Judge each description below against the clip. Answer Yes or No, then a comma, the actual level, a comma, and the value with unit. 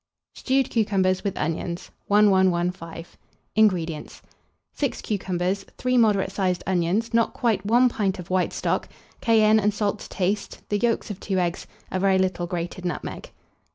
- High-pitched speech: Yes, high, 195 Hz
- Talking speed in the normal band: Yes, average, 150 wpm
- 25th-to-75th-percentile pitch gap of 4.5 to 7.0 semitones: No, average, 3.2 semitones